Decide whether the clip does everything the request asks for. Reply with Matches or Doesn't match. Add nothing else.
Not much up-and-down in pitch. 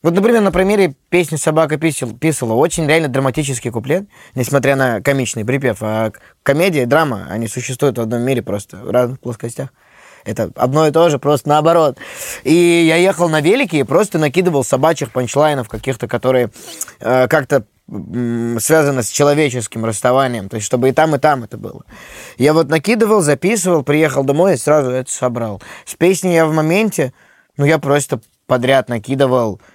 Doesn't match